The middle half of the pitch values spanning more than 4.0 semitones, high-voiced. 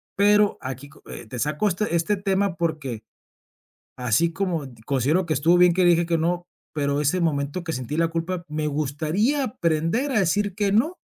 No: average, 4.6 semitones; medium, 170 Hz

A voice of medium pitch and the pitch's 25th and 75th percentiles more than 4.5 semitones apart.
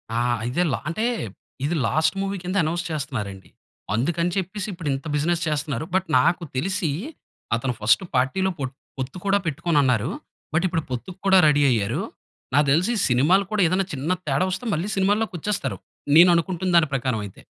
Yes: medium, 160 Hz; wide, 5.6 semitones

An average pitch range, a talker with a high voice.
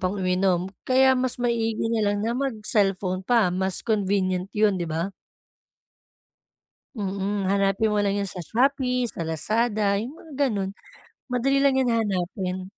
Yes: average, 4.0 semitones; high, 205 Hz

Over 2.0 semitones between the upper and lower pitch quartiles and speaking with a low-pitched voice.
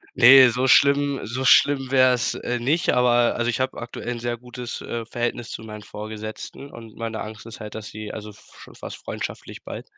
Yes: narrow, 2.6 semitones; low, 120 Hz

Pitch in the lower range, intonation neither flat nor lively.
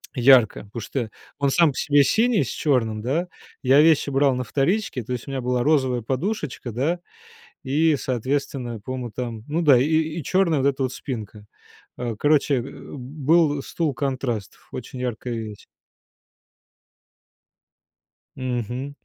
Yes: low, 130 Hz; average, 3.3 semitones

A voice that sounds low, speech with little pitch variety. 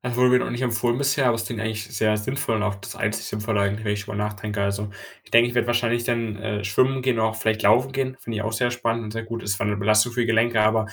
Yes: low, 110 Hz; narrow, 2.3 semitones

